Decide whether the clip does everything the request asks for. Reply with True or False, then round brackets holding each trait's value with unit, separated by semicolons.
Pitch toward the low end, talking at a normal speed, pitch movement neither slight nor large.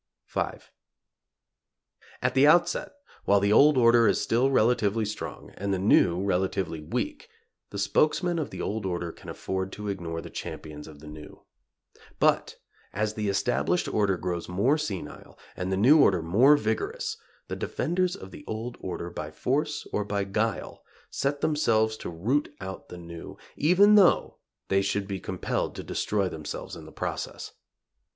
False (105 Hz; 160 wpm; 7.1 semitones)